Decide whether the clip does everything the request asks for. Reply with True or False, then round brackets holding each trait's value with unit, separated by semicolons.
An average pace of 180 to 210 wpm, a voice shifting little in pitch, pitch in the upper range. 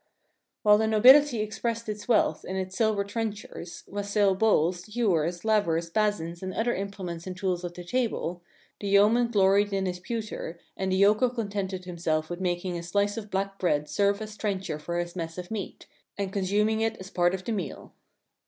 False (195 wpm; 3.2 semitones; 195 Hz)